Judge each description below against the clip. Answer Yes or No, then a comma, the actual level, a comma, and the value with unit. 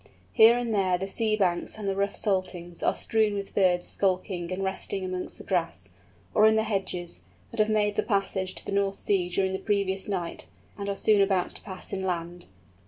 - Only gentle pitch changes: Yes, narrow, 2.0 semitones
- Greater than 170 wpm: Yes, fast, 205 wpm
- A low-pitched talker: No, high, 195 Hz